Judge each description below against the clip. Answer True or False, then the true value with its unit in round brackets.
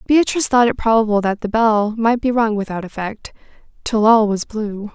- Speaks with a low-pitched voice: False (220 Hz)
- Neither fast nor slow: True (195 wpm)